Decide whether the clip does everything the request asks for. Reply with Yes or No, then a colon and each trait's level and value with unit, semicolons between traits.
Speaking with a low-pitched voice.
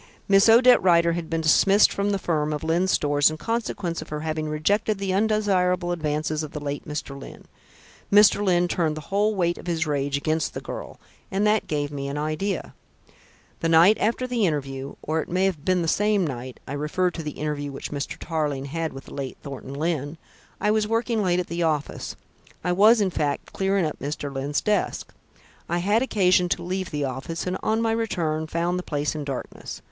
No: medium, 165 Hz